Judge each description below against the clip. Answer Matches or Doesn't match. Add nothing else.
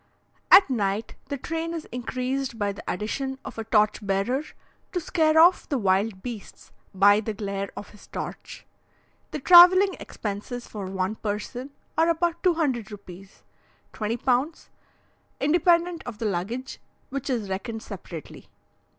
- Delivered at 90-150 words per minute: Matches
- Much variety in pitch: Matches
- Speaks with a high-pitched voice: Matches